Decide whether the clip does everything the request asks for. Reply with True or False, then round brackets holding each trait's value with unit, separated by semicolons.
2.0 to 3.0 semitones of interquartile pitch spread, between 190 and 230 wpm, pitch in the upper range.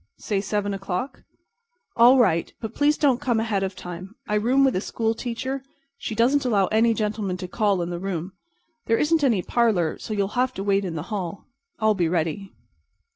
False (4.0 semitones; 200 wpm; 210 Hz)